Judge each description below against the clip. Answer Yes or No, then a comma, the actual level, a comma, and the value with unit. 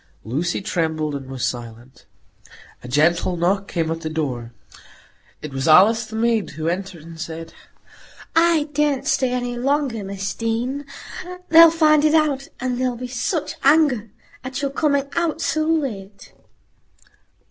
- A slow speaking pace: No, average, 145 wpm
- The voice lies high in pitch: Yes, high, 225 Hz